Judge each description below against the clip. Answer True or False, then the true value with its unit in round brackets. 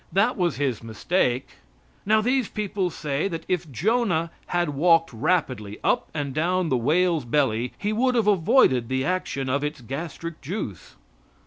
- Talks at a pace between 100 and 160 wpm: True (155 wpm)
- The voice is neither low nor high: True (165 Hz)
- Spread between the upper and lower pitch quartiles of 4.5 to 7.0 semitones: True (5.5 semitones)